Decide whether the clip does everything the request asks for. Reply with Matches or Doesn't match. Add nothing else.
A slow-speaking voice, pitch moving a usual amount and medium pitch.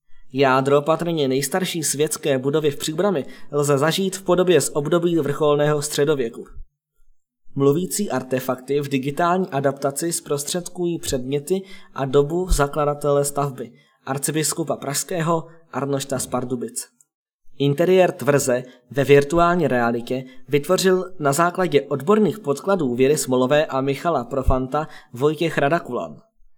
Matches